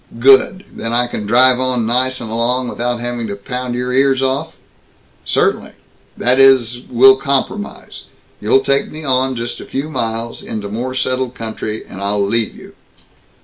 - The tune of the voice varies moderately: No, narrow, 2.3 semitones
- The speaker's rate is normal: Yes, average, 165 wpm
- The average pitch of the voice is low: Yes, low, 125 Hz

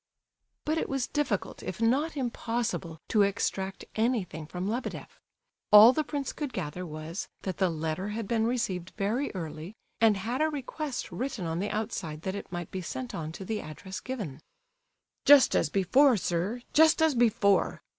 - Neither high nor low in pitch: No, high, 210 Hz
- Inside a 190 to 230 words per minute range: No, average, 170 wpm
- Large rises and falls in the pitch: Yes, wide, 5.8 semitones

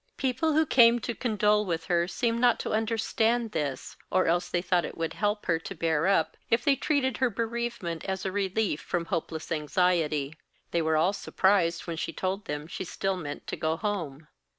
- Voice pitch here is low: No, medium, 185 Hz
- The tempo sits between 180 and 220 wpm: Yes, average, 195 wpm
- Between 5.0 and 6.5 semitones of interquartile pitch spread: Yes, average, 5.3 semitones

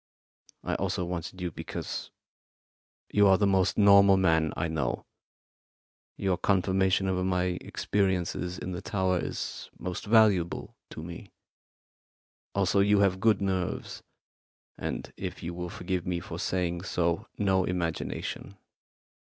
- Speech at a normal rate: No, slow, 130 wpm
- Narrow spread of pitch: Yes, narrow, 1.9 semitones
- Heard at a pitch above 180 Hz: No, very low, 95 Hz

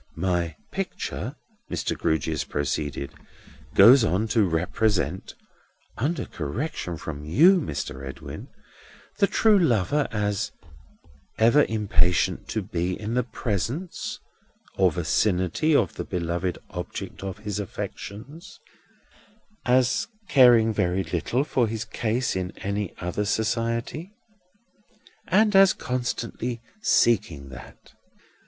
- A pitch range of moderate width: No, wide, 5.9 semitones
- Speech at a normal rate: No, slow, 105 wpm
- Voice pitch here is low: Yes, low, 105 Hz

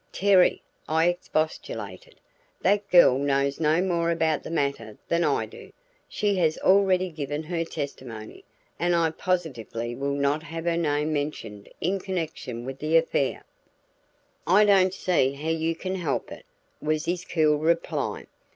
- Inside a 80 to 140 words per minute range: No, average, 150 wpm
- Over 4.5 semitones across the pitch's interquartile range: No, average, 3.7 semitones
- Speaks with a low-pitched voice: No, medium, 160 Hz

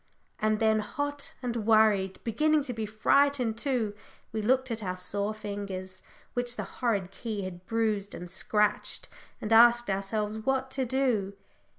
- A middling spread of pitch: Yes, average, 3.2 semitones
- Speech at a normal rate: Yes, average, 155 wpm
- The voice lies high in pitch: Yes, high, 220 Hz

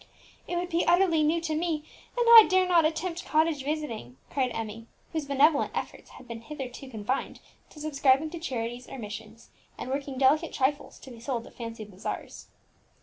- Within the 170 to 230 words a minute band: Yes, average, 180 wpm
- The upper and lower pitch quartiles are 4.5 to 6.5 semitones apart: Yes, average, 5.3 semitones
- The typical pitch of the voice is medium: No, very high, 280 Hz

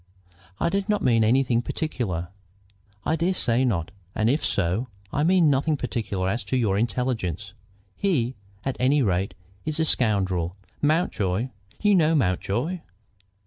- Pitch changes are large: Yes, wide, 7.5 semitones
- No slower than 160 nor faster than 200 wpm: No, average, 145 wpm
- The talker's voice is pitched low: Yes, low, 125 Hz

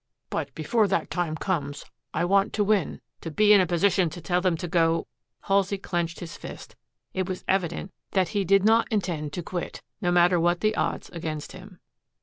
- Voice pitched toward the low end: No, medium, 180 Hz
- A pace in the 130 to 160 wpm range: No, average, 200 wpm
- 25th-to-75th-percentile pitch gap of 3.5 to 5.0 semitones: No, average, 2.9 semitones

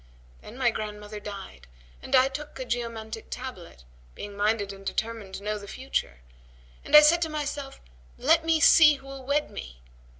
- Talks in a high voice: Yes, high, 230 Hz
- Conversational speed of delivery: Yes, average, 175 wpm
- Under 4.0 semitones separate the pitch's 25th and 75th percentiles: No, wide, 5.4 semitones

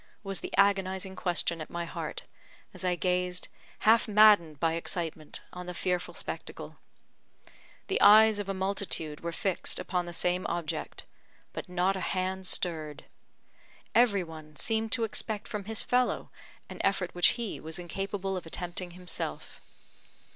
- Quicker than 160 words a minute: No, average, 150 wpm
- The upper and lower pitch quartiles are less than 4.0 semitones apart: Yes, narrow, 2.6 semitones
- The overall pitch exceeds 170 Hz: Yes, medium, 185 Hz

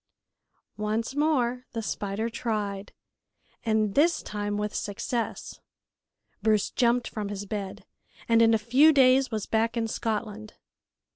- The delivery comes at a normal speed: No, slow, 130 wpm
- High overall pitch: Yes, high, 225 Hz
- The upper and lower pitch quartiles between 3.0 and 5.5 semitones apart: No, narrow, 2.4 semitones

